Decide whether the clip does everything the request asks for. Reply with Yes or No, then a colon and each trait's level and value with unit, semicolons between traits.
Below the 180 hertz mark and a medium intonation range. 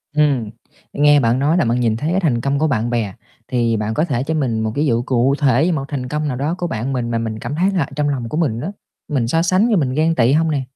Yes: medium, 140 Hz; average, 4.6 semitones